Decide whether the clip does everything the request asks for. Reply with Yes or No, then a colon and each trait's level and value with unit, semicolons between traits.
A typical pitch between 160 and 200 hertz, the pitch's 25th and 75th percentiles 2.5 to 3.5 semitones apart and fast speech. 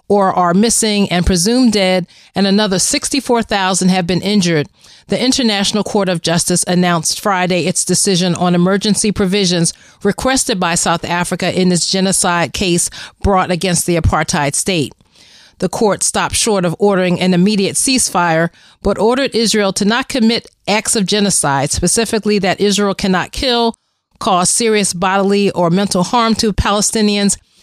No: high, 190 Hz; average, 2.8 semitones; average, 150 wpm